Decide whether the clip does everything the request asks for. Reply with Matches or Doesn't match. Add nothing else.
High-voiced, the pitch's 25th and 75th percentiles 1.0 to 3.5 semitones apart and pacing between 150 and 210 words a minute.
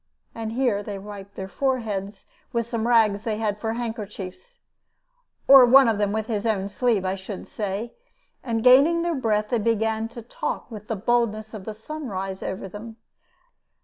Matches